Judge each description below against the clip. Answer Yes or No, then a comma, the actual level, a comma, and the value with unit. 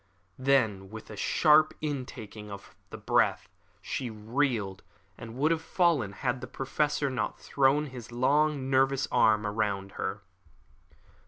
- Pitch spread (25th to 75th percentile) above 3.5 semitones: Yes, average, 4.8 semitones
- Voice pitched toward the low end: Yes, low, 130 Hz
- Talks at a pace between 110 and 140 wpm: Yes, slow, 135 wpm